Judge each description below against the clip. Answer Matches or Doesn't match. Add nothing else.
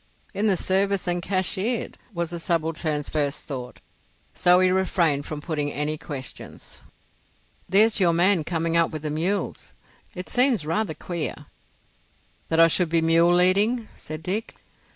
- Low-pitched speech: Doesn't match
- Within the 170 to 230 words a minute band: Doesn't match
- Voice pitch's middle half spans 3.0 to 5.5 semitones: Matches